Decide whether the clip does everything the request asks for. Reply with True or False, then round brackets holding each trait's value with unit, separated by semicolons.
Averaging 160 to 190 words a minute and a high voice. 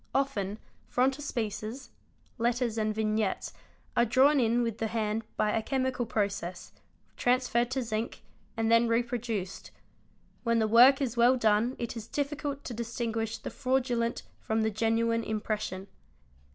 False (140 wpm; 230 Hz)